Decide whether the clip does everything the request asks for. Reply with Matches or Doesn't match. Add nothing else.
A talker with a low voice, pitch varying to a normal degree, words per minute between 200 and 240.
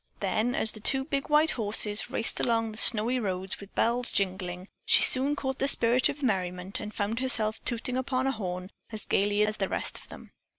Doesn't match